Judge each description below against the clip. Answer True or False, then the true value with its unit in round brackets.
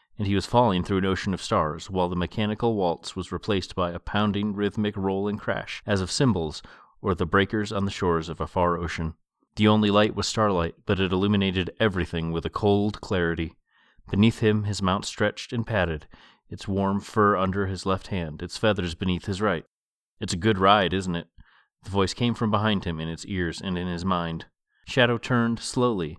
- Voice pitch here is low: True (95 Hz)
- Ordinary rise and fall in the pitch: True (3.1 semitones)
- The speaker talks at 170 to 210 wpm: True (205 wpm)